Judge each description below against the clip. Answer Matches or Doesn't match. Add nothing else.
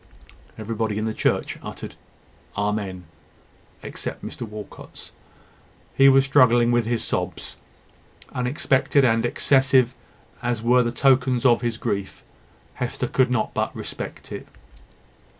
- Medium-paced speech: Doesn't match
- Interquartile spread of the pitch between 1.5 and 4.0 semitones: Matches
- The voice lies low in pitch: Matches